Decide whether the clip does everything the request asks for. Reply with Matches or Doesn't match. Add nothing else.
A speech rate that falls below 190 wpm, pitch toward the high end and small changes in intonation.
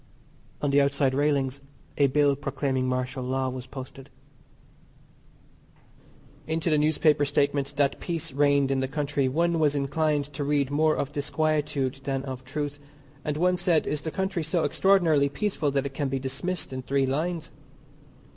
Doesn't match